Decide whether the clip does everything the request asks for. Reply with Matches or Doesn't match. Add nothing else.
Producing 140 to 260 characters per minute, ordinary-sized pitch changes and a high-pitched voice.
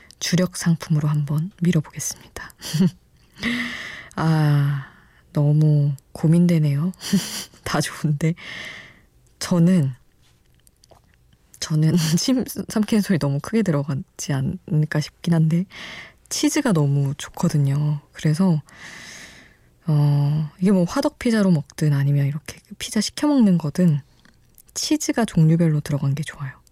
Doesn't match